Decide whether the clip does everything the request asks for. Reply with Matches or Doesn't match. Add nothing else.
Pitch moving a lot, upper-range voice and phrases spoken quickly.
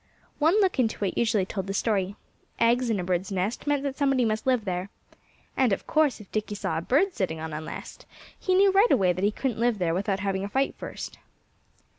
Matches